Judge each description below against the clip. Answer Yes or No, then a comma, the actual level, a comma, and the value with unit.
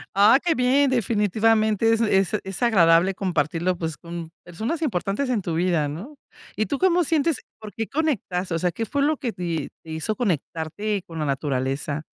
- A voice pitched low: No, high, 195 Hz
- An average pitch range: No, wide, 6.2 semitones